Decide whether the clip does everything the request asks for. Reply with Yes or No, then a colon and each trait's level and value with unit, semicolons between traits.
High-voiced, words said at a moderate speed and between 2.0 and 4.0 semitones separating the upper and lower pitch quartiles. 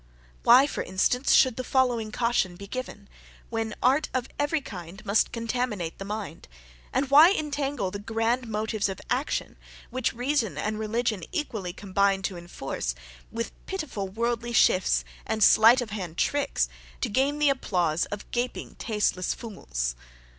No: high, 225 Hz; average, 150 wpm; average, 4.4 semitones